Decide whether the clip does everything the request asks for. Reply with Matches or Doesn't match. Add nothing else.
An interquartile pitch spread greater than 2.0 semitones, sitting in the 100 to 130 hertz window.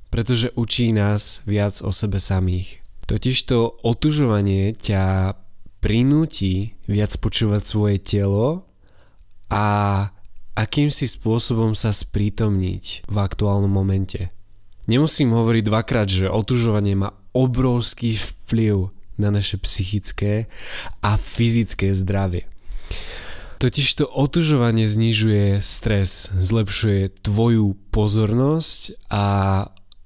Matches